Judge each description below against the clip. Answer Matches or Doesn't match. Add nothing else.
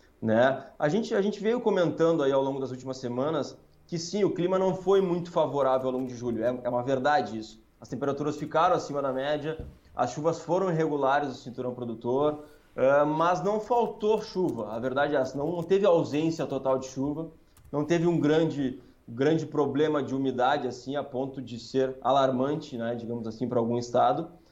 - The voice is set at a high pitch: Doesn't match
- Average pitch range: Matches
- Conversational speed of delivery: Doesn't match